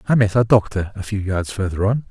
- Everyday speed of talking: No, fast, 255 wpm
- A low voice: Yes, low, 105 Hz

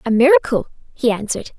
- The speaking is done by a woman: Yes, female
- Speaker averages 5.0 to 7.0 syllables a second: Yes, 6.5 syllables/s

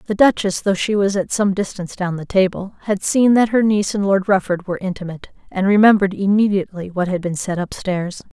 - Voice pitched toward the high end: Yes, high, 195 Hz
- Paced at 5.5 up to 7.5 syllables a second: Yes, 5.9 syllables/s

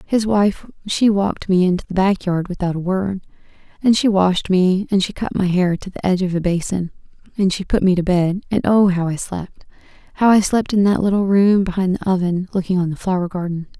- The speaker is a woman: Yes, female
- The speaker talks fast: Yes, fast, 225 wpm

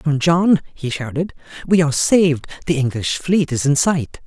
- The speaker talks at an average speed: Yes, average, 185 wpm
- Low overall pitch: No, medium, 155 Hz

